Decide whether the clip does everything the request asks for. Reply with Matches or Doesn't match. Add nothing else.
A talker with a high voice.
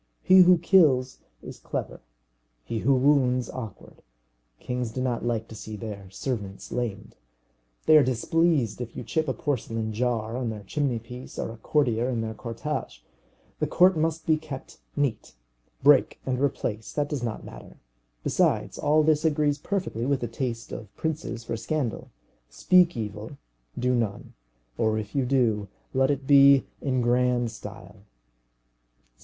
Doesn't match